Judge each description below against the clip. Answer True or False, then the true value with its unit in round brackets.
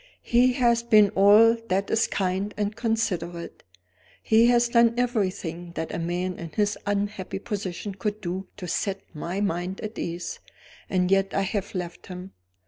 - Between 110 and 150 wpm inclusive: False (160 wpm)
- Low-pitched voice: False (195 Hz)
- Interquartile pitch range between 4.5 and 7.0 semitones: False (3.3 semitones)